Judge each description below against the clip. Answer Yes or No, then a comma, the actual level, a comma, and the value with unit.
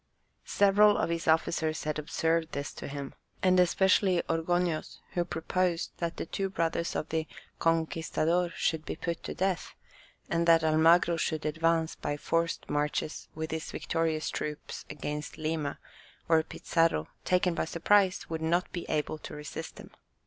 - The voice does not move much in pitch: Yes, narrow, 1.7 semitones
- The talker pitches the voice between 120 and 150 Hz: No, medium, 165 Hz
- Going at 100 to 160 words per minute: Yes, average, 155 wpm